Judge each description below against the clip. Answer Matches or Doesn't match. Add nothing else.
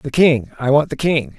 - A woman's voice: Doesn't match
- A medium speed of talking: Doesn't match